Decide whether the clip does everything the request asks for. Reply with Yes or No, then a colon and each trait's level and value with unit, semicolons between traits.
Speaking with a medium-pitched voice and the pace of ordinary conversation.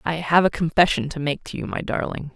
No: medium, 155 Hz; fast, 255 wpm